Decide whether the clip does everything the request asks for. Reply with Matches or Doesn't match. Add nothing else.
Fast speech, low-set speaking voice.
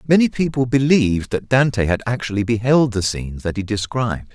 Doesn't match